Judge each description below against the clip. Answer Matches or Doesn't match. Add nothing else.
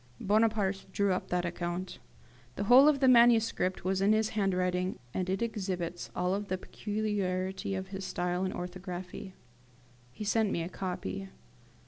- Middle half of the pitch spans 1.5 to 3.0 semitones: Matches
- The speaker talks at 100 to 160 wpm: Matches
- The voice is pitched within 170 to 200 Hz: Matches